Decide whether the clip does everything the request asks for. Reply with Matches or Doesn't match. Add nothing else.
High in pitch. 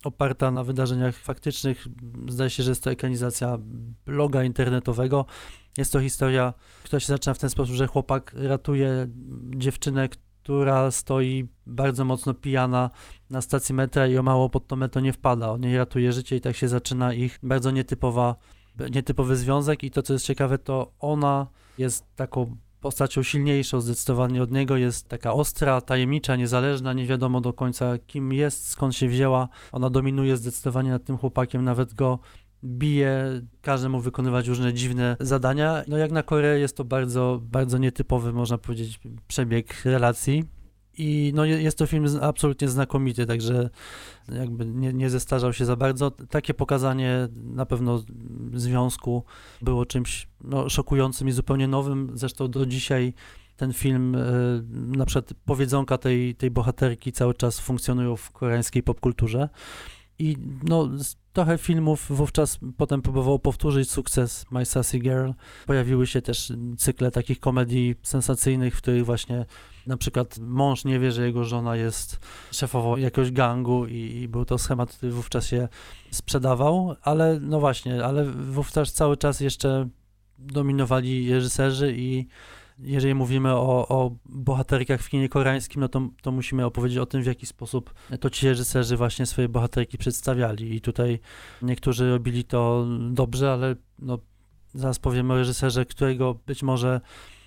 Doesn't match